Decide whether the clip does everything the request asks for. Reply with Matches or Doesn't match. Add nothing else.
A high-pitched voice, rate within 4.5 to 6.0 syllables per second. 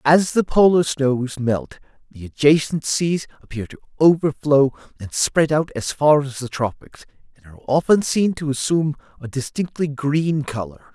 Doesn't match